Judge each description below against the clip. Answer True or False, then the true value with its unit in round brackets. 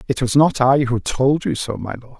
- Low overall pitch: True (130 Hz)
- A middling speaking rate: False (275 wpm)